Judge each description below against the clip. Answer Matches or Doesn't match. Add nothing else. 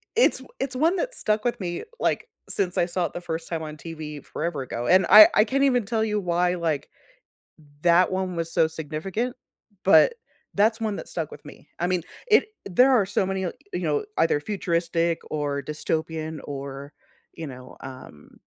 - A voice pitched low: Doesn't match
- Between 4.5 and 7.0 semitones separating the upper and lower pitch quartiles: Matches